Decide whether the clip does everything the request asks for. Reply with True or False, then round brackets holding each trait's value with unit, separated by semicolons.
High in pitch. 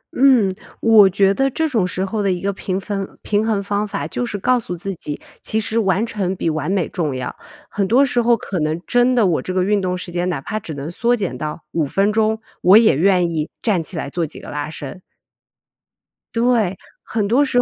True (195 Hz)